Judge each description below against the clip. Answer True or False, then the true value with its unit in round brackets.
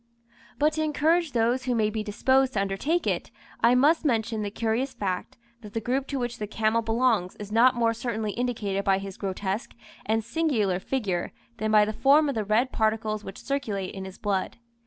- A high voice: True (225 Hz)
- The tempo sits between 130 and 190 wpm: False (200 wpm)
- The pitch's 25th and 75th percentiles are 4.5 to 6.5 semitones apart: False (3.8 semitones)